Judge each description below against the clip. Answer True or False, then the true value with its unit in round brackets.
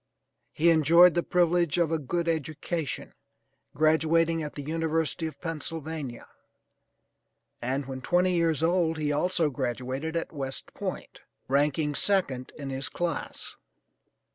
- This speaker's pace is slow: True (125 wpm)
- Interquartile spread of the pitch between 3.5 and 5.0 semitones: False (2.9 semitones)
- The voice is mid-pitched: True (160 Hz)